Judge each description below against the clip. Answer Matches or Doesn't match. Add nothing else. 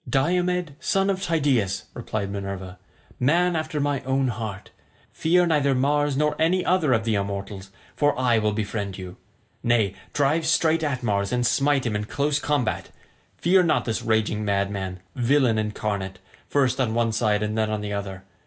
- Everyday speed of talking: Matches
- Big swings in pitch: Matches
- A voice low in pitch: Matches